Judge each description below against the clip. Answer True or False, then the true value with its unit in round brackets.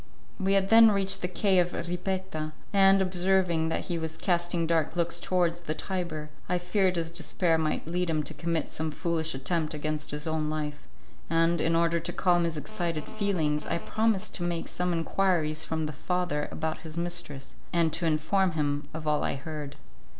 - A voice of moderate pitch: True (170 Hz)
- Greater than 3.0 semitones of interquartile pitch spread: False (2.5 semitones)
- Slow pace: False (185 wpm)